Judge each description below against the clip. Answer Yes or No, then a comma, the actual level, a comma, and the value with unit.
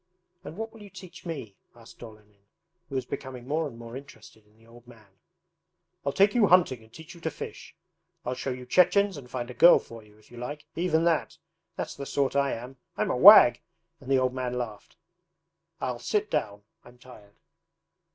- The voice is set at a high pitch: No, low, 130 Hz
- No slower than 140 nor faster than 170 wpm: No, average, 200 wpm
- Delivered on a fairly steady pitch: No, wide, 5.6 semitones